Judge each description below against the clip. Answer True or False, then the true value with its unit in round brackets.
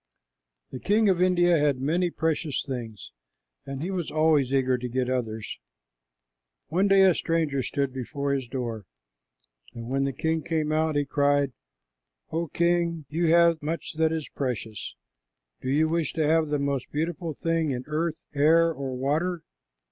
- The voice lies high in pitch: False (150 Hz)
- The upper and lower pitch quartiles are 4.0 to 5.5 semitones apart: False (3.6 semitones)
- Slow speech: False (165 wpm)